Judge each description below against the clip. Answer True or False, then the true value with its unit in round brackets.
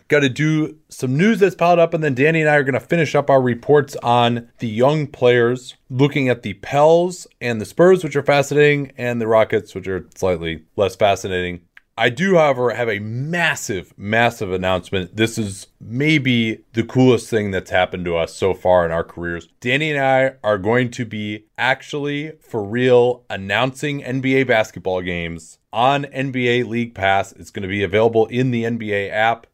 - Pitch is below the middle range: True (120 Hz)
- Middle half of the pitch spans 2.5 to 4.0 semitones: False (5.6 semitones)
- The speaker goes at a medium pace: True (185 wpm)